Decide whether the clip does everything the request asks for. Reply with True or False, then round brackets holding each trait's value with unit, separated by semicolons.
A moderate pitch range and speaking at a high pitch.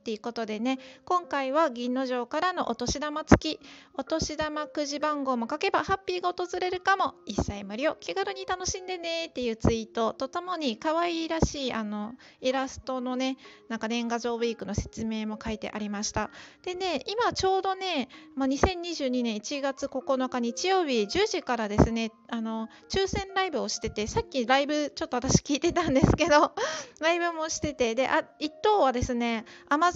False (6.3 semitones; 280 Hz)